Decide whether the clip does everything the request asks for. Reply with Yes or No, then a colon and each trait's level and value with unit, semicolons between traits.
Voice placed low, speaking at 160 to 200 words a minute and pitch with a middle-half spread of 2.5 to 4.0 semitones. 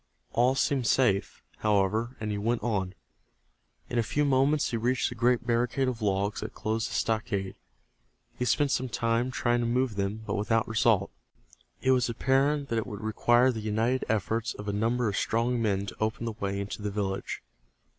Yes: low, 115 Hz; average, 190 wpm; average, 2.9 semitones